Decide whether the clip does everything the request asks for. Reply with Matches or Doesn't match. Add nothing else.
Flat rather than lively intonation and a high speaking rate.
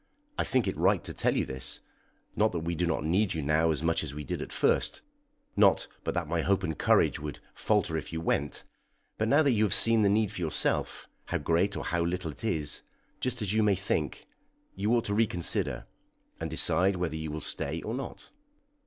Doesn't match